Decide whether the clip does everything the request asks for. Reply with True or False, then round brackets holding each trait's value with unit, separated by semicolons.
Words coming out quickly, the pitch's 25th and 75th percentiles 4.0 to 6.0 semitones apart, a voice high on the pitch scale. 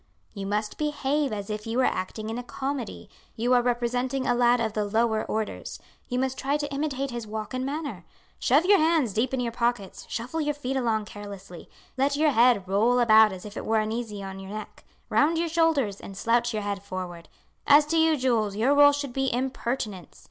True (210 wpm; 4.4 semitones; 240 Hz)